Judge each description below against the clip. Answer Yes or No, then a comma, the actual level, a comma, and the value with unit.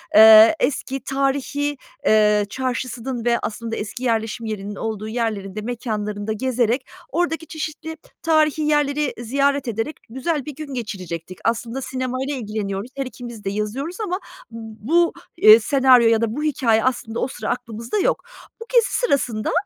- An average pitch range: Yes, average, 4.4 semitones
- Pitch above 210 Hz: Yes, high, 245 Hz